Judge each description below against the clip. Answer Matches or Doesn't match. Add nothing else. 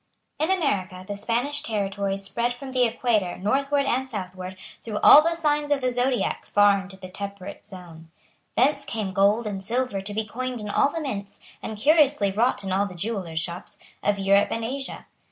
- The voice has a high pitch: Matches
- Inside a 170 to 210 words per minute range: Matches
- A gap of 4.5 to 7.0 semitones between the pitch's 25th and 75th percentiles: Matches